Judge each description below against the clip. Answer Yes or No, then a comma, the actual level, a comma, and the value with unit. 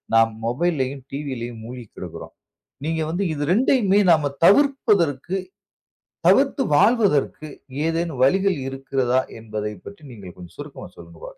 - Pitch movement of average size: No, wide, 7.7 semitones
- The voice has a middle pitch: Yes, medium, 145 Hz